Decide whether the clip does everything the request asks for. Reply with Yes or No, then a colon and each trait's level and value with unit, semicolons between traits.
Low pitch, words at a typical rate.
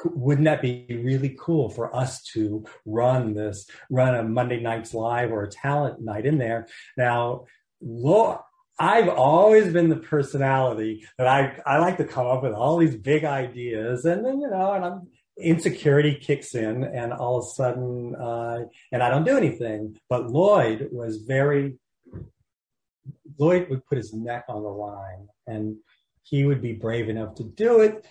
Yes: low, 125 Hz; average, 175 wpm